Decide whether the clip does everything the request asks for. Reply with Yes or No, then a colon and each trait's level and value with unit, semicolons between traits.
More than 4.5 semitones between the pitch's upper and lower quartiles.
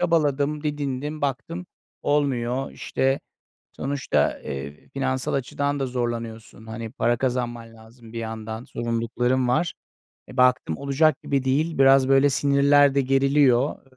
No: average, 3.1 semitones